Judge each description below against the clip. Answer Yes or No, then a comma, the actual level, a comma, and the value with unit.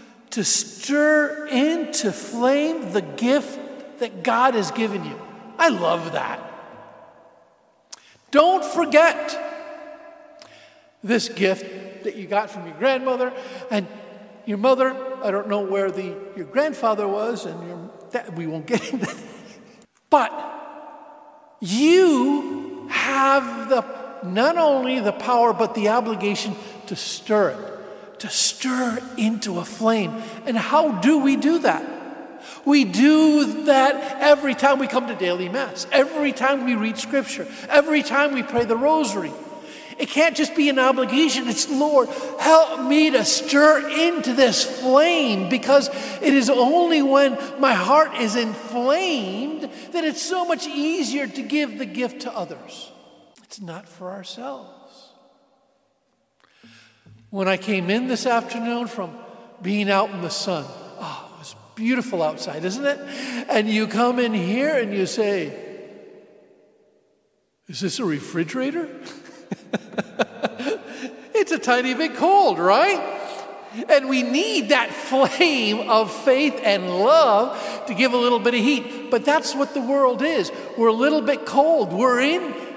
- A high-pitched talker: Yes, very high, 260 Hz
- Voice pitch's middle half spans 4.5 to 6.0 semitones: Yes, average, 5.1 semitones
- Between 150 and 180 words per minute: No, average, 140 wpm